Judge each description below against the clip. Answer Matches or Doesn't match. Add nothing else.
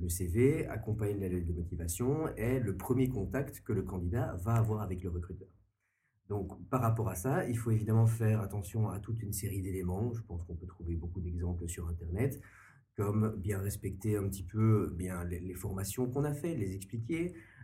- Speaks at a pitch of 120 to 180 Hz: Doesn't match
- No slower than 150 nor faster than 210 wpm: Matches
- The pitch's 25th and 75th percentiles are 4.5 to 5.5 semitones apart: Doesn't match